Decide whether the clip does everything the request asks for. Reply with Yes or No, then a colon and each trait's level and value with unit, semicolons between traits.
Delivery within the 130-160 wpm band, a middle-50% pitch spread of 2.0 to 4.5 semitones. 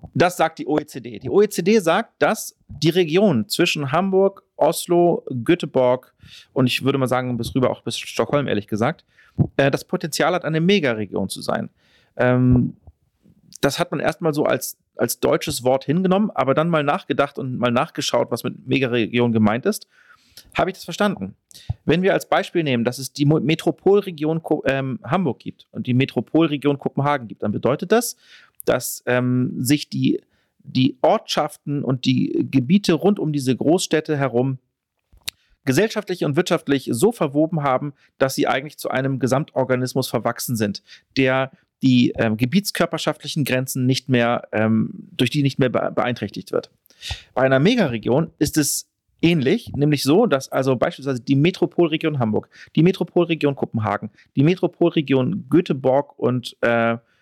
No: average, 150 wpm; average, 5.0 semitones